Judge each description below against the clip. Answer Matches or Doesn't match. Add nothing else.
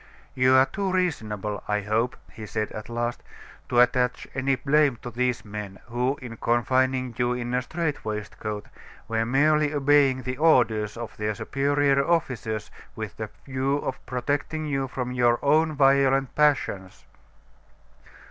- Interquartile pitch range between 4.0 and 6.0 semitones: Doesn't match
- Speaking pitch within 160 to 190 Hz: Doesn't match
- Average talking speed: Matches